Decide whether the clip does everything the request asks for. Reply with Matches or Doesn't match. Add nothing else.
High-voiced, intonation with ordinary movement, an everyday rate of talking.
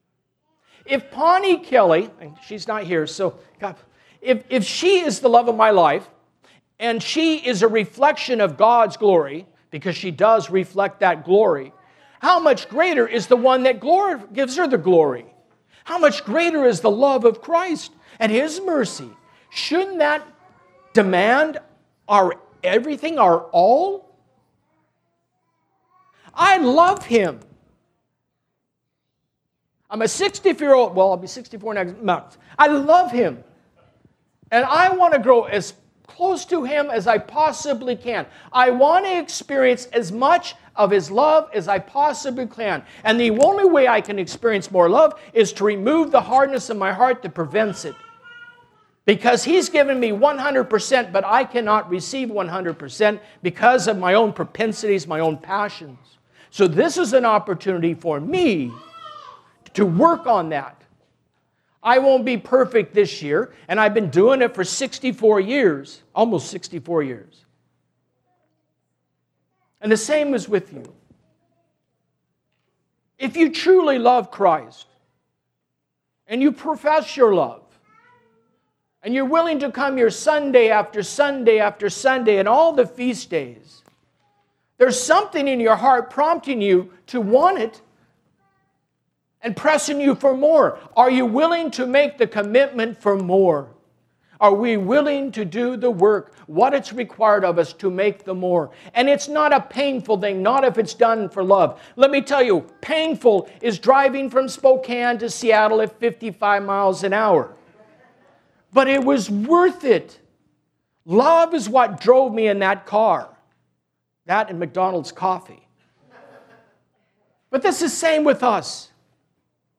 Doesn't match